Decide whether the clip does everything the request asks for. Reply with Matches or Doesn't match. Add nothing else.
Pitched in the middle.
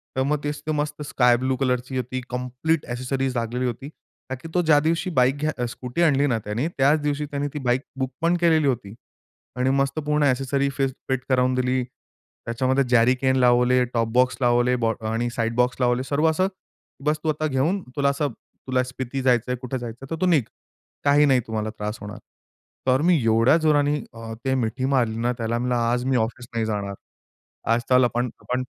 Doesn't match